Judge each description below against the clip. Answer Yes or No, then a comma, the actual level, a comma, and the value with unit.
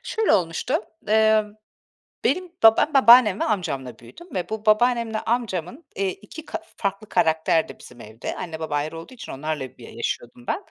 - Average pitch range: No, wide, 6.9 semitones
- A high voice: Yes, high, 205 Hz